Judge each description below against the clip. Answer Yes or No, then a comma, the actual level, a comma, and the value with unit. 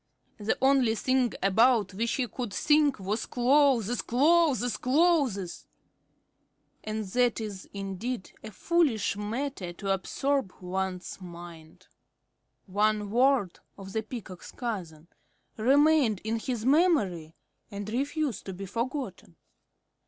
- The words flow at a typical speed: No, slow, 115 wpm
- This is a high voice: Yes, high, 220 Hz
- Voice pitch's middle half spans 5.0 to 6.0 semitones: Yes, wide, 5.4 semitones